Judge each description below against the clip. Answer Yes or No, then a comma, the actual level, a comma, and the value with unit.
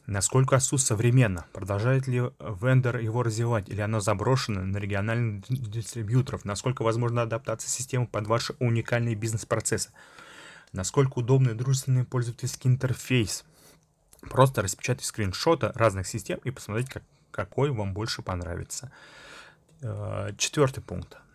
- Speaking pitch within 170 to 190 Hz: No, low, 115 Hz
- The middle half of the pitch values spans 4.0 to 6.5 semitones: No, average, 3.4 semitones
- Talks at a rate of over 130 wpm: No, slow, 110 wpm